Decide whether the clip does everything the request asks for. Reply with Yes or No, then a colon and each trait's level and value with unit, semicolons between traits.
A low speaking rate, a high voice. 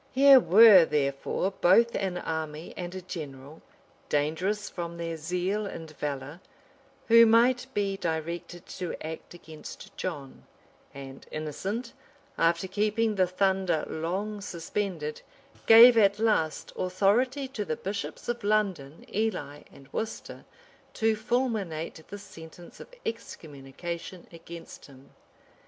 No: slow, 120 wpm; medium, 180 Hz